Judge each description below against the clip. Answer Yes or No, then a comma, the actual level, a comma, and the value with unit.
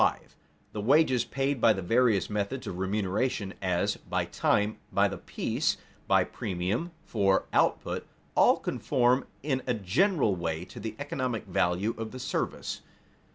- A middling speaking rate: Yes, average, 145 wpm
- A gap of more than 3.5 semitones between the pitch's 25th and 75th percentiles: Yes, average, 5.1 semitones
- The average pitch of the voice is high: No, low, 110 Hz